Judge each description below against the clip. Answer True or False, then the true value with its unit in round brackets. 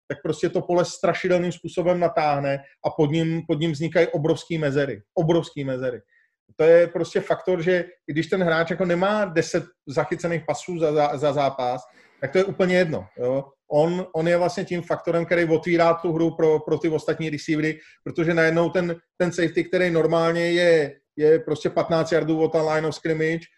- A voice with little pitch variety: True (2.1 semitones)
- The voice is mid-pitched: True (165 Hz)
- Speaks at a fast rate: True (185 wpm)